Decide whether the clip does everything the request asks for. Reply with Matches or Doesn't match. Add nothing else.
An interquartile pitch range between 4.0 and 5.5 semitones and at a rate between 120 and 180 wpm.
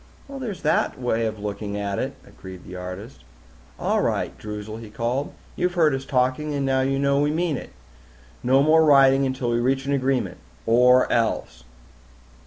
Matches